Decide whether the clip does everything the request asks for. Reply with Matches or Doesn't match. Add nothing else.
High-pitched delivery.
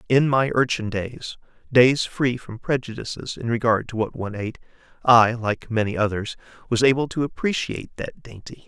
Doesn't match